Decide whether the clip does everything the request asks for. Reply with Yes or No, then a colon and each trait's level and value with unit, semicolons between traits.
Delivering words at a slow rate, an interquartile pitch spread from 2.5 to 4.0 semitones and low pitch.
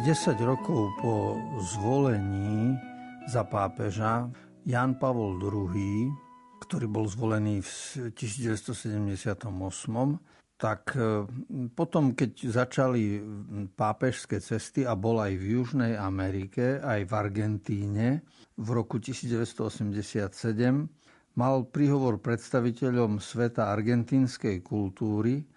Yes: slow, 90 wpm; average, 3.5 semitones; low, 115 Hz